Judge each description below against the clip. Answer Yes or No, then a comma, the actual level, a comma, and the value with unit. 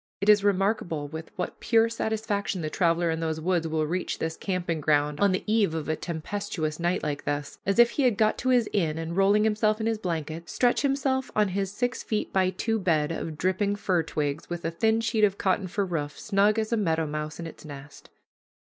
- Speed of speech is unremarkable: No, fast, 220 wpm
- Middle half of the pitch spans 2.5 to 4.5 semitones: No, average, 4.9 semitones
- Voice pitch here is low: No, medium, 185 Hz